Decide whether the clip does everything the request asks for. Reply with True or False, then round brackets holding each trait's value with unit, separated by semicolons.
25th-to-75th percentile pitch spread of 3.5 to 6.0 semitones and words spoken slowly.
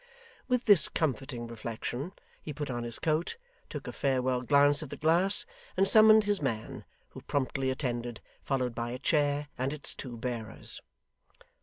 False (4.3 semitones; 160 wpm)